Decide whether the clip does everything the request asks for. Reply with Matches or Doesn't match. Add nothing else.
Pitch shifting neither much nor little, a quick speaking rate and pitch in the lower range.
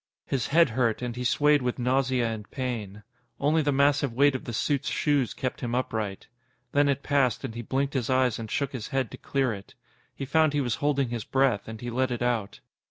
Matches